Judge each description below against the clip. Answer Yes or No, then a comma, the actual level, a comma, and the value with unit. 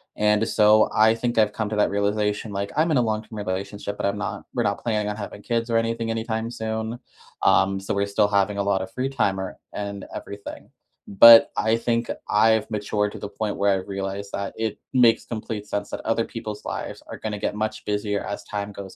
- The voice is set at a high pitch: No, low, 105 Hz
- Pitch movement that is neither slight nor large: No, narrow, 1.7 semitones